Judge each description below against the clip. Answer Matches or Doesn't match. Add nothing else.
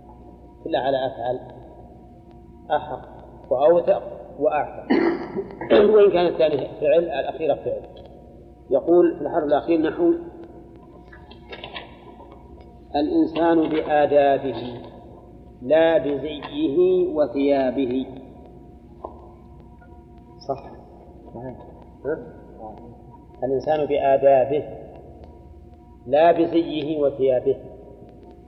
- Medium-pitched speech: Matches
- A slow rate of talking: Matches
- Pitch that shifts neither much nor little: Doesn't match